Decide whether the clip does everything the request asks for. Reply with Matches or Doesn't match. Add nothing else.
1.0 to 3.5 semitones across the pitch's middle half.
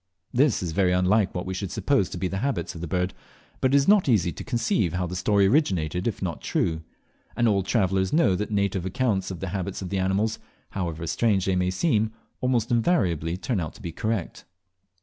Doesn't match